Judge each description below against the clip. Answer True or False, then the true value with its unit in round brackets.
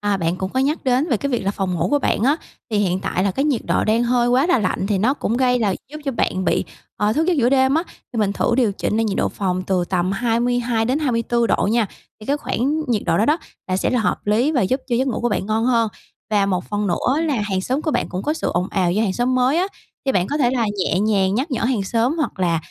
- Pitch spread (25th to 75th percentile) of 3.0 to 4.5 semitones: False (4.9 semitones)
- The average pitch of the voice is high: True (230 Hz)